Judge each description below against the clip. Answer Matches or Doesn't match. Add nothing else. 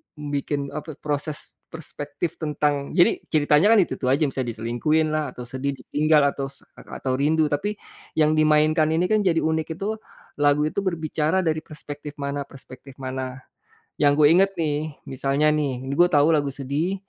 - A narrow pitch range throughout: Matches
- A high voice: Doesn't match